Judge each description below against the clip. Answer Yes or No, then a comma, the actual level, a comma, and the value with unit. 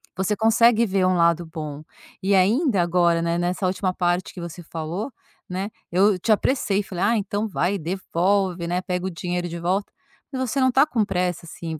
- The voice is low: No, medium, 185 Hz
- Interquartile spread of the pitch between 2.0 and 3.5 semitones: Yes, average, 2.9 semitones